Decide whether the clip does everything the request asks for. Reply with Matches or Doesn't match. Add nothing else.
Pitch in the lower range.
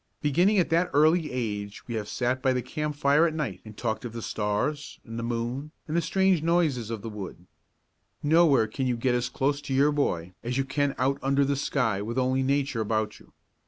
Matches